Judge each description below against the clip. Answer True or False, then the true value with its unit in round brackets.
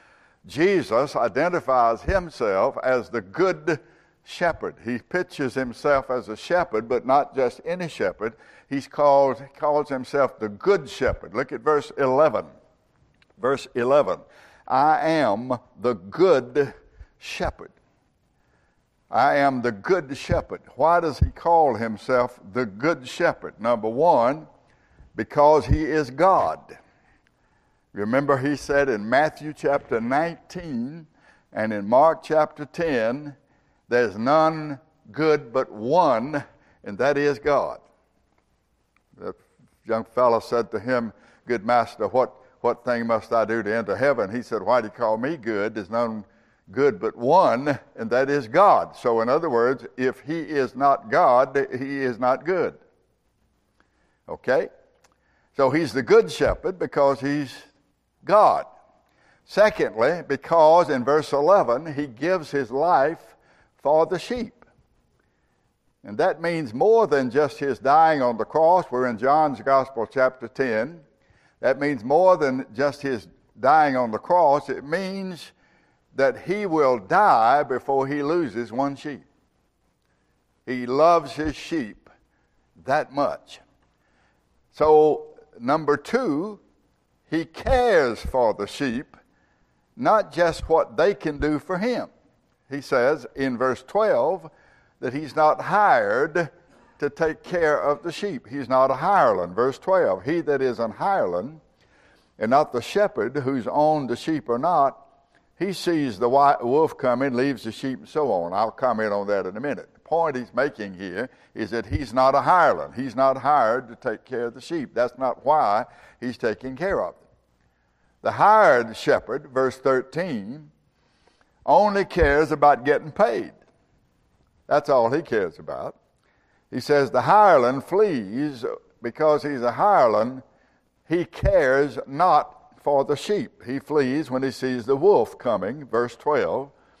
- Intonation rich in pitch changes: False (4.8 semitones)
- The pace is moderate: True (145 wpm)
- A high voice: False (140 Hz)